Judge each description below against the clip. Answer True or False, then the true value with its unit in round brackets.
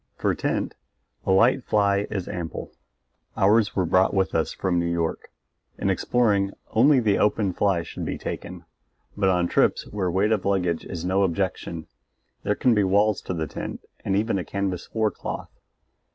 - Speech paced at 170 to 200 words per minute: True (175 wpm)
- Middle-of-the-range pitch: False (95 Hz)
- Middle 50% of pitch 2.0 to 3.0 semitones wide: True (2.7 semitones)